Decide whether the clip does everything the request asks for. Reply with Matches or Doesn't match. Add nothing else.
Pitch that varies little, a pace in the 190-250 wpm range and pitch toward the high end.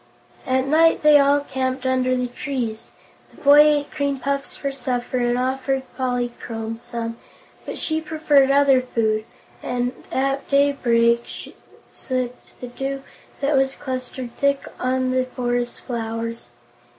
Doesn't match